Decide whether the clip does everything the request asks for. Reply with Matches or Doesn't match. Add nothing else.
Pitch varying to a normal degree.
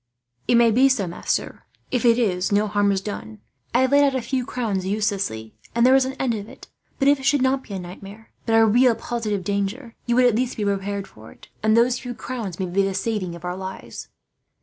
Matches